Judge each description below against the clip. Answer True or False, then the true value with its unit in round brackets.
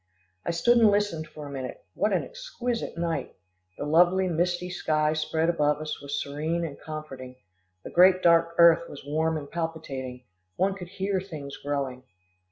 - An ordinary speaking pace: True (170 wpm)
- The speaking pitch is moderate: True (160 Hz)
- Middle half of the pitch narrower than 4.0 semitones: True (3.3 semitones)